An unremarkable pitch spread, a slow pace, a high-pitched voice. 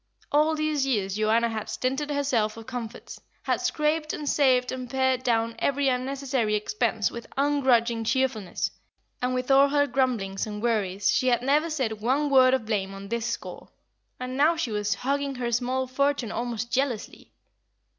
No: average, 3.6 semitones; average, 165 wpm; very high, 255 Hz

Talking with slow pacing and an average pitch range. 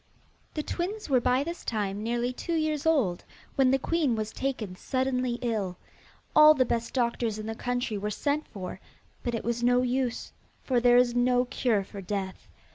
No: average, 185 wpm; average, 3.4 semitones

